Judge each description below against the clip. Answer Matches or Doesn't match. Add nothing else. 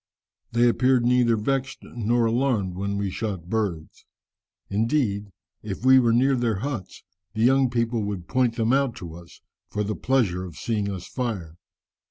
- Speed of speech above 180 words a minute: Doesn't match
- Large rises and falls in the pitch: Doesn't match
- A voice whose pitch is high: Doesn't match